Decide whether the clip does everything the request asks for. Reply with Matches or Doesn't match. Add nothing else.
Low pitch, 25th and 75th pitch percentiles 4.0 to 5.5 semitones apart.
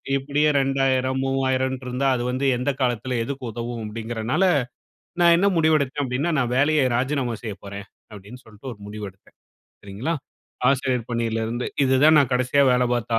Doesn't match